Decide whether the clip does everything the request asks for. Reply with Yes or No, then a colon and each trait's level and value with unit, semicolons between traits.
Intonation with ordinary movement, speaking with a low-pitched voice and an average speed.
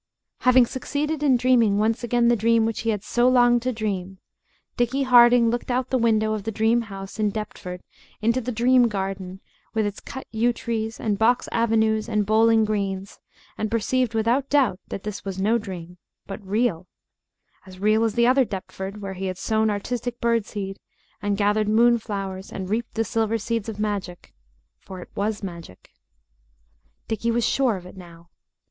No: average, 3.1 semitones; high, 220 Hz; average, 180 wpm